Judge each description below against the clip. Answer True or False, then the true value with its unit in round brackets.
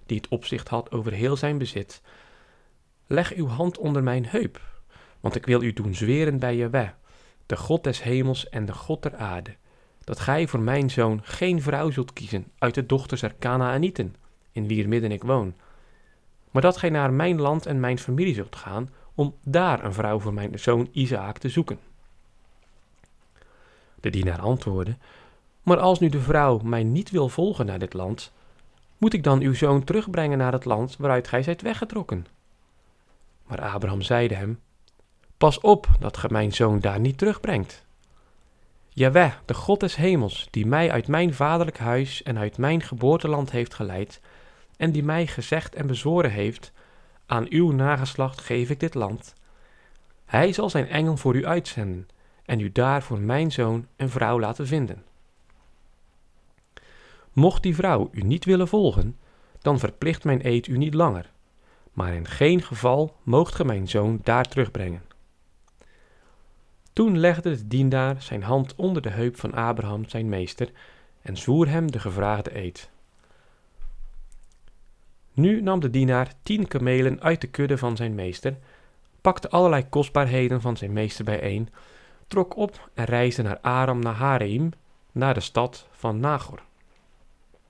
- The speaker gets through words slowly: False (160 wpm)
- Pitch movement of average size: False (5.7 semitones)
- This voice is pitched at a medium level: False (125 Hz)